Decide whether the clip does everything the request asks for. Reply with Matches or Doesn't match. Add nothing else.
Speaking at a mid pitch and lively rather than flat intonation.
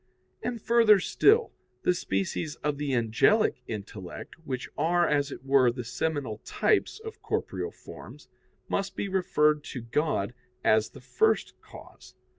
Matches